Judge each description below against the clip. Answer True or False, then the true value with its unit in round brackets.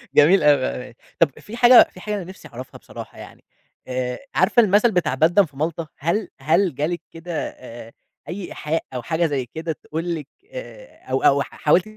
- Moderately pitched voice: True (165 Hz)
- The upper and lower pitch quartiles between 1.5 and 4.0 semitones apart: False (5.2 semitones)